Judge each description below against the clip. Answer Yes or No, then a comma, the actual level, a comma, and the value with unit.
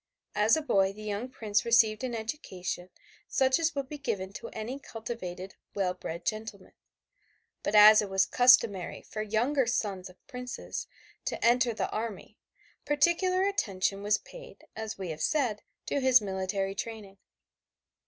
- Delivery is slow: No, average, 155 wpm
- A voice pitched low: No, high, 215 Hz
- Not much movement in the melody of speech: No, average, 4.2 semitones